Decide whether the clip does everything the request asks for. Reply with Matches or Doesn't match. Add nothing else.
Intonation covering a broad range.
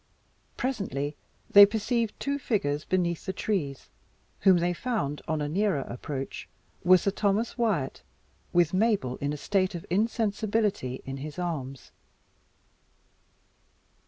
Matches